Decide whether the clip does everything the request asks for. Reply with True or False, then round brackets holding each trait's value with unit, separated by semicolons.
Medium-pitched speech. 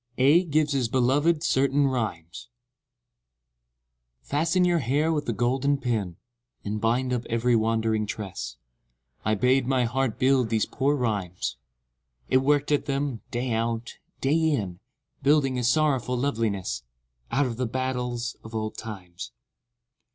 False (125 Hz)